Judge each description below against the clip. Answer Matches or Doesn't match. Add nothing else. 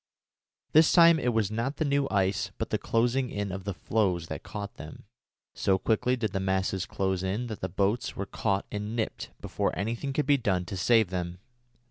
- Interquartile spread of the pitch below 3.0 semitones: Doesn't match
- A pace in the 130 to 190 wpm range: Doesn't match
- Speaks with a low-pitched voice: Matches